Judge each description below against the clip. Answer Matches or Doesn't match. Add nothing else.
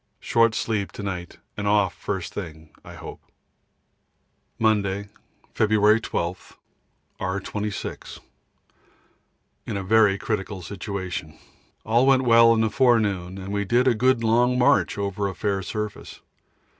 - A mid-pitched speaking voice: Doesn't match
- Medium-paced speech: Doesn't match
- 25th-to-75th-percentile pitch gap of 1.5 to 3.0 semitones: Matches